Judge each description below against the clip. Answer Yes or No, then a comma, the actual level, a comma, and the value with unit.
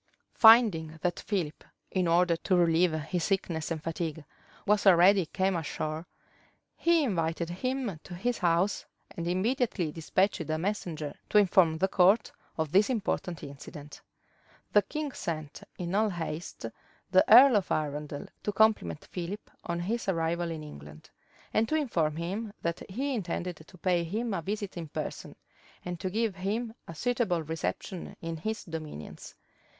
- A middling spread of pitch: Yes, average, 4.3 semitones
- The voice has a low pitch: No, medium, 175 Hz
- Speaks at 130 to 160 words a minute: Yes, average, 155 wpm